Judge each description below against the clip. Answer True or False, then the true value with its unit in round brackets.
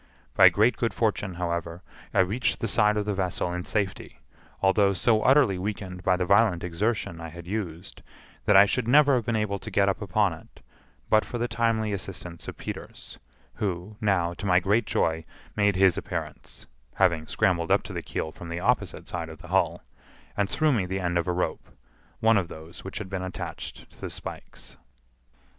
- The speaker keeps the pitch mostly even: False (3.4 semitones)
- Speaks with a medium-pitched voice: False (95 Hz)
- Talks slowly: False (190 wpm)